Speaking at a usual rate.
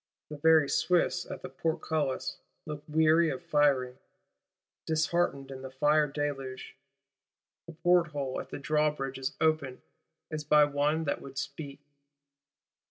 No: slow, 130 wpm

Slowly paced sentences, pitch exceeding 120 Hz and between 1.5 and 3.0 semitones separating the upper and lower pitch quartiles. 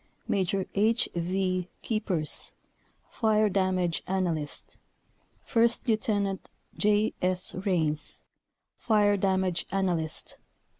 Yes: slow, 85 wpm; high, 190 Hz; average, 2.7 semitones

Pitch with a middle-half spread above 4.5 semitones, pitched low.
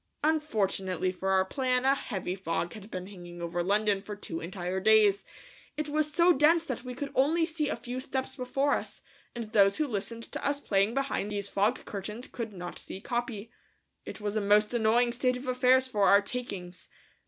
No: average, 4.9 semitones; high, 220 Hz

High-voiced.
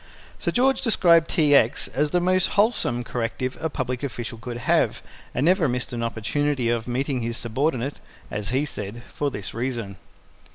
No: low, 130 Hz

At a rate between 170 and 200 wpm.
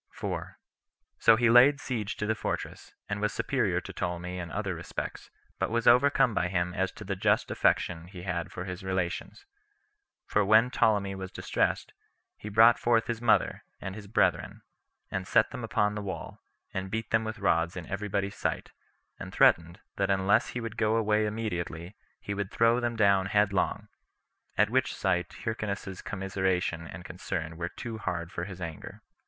Yes: average, 175 wpm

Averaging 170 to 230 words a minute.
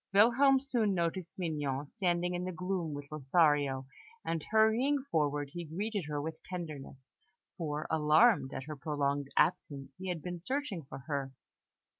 No: average, 150 wpm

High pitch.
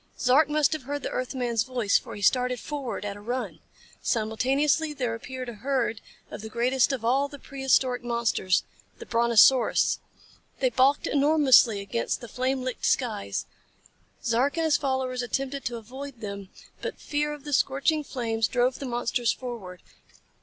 Yes: very high, 255 Hz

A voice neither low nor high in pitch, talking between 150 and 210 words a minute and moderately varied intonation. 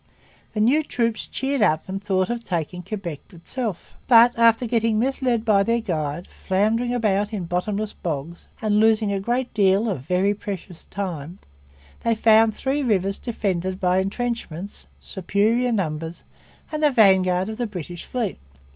No: high, 205 Hz; average, 155 wpm; average, 3.9 semitones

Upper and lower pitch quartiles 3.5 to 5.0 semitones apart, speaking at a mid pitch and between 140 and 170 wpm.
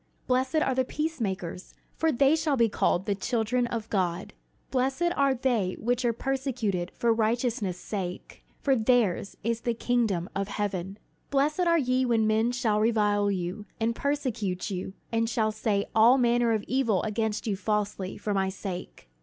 No: average, 3.9 semitones; high, 225 Hz; average, 165 wpm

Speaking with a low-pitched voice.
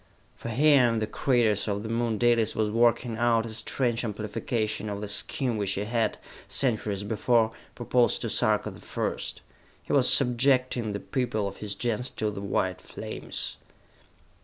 Yes: low, 115 Hz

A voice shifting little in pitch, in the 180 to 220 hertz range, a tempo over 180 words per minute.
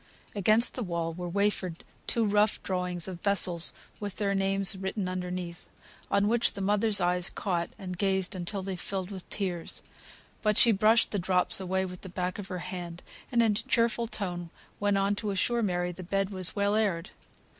Yes: narrow, 2.3 semitones; high, 190 Hz; average, 190 wpm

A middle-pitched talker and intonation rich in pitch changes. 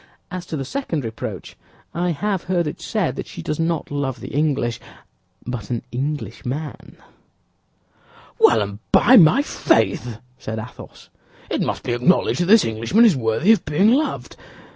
Yes: medium, 145 Hz; wide, 7.0 semitones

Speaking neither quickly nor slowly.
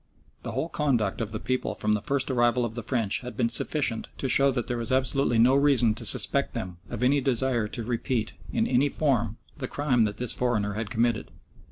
No: fast, 215 wpm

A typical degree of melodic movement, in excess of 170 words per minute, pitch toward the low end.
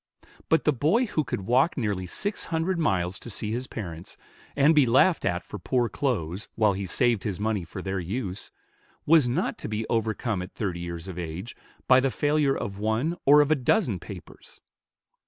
No: wide, 7.0 semitones; average, 190 wpm; low, 110 Hz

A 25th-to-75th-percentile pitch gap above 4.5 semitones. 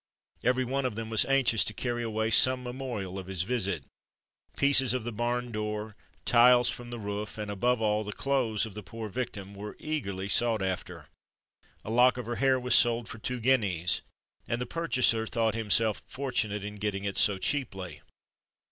No: average, 3.2 semitones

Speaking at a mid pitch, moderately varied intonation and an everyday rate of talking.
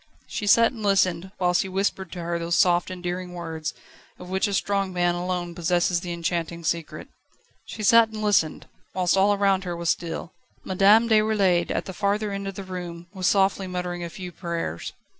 No: medium, 180 Hz; narrow, 2.3 semitones; average, 190 wpm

